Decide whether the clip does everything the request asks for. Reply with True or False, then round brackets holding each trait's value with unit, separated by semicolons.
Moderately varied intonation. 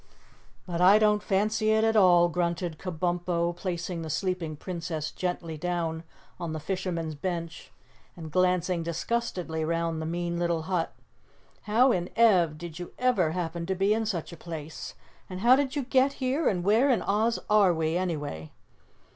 True (3.6 semitones)